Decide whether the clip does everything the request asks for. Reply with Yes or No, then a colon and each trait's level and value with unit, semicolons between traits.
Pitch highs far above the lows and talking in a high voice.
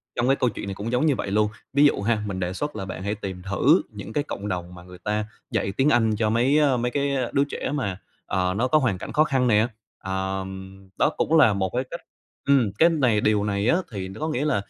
No: wide, 5.9 semitones; low, 110 Hz